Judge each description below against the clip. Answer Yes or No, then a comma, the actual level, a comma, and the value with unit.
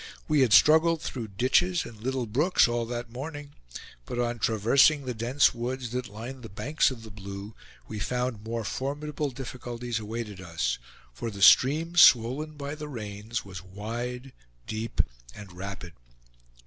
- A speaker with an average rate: Yes, average, 155 wpm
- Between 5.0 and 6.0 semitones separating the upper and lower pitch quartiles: No, average, 4.0 semitones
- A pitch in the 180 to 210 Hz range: No, low, 120 Hz